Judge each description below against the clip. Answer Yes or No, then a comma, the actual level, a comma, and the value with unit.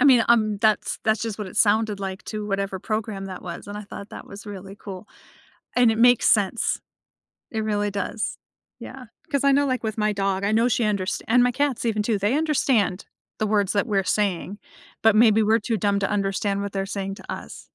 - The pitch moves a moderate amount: No, narrow, 2.2 semitones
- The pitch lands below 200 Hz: No, high, 210 Hz